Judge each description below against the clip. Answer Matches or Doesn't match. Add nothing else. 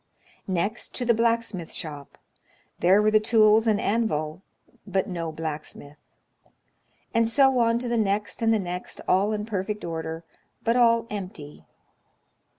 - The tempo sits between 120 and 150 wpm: Matches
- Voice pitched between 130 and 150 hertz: Doesn't match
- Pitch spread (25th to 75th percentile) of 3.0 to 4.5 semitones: Doesn't match